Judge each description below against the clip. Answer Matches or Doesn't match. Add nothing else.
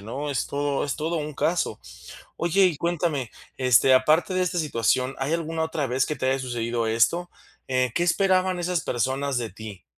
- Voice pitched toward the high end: Doesn't match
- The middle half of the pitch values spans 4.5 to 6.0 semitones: Matches